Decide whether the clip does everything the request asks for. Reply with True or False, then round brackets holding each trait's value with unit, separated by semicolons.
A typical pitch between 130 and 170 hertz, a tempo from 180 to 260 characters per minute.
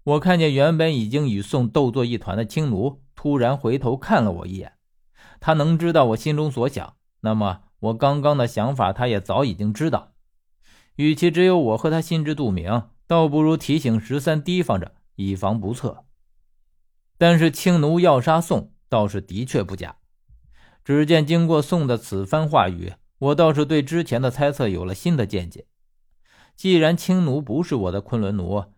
True (135 Hz; 255 characters per minute)